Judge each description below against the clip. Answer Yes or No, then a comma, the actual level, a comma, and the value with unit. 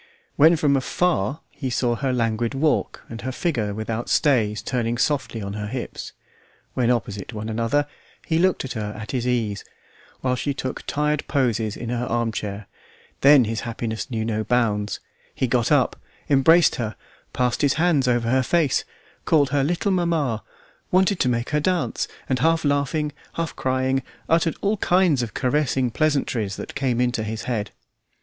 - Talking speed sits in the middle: Yes, average, 170 wpm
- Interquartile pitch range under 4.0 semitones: No, average, 4.5 semitones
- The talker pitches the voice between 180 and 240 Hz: No, low, 125 Hz